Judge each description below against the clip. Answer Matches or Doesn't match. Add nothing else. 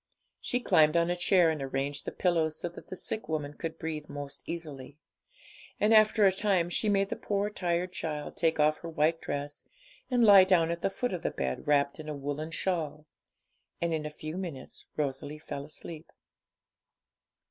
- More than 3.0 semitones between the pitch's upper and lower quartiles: Matches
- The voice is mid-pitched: Matches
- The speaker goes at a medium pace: Matches